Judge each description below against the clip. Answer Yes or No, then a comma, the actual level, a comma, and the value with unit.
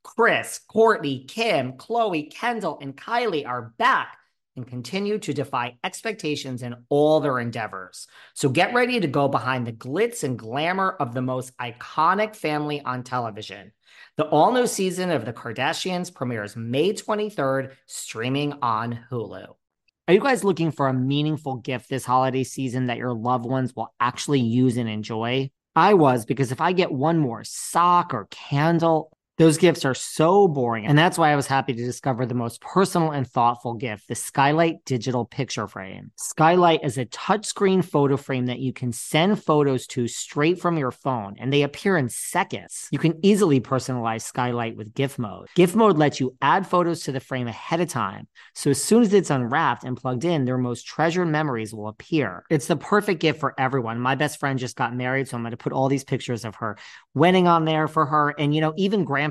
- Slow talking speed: No, average, 190 wpm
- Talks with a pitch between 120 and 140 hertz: Yes, low, 135 Hz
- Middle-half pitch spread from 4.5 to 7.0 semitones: Yes, average, 4.9 semitones